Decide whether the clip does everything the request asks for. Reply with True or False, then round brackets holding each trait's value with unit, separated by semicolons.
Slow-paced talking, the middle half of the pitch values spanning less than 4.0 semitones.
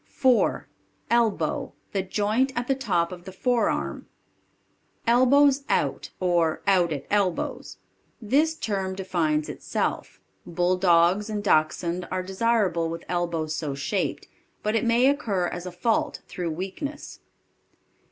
False (125 wpm; 5.1 semitones)